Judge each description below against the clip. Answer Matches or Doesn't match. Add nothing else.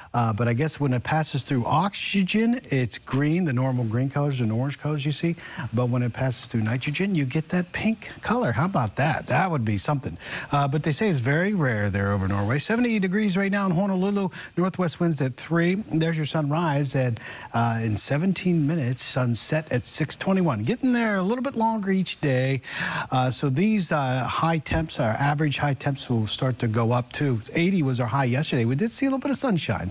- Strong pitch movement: Matches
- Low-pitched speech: Doesn't match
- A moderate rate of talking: Doesn't match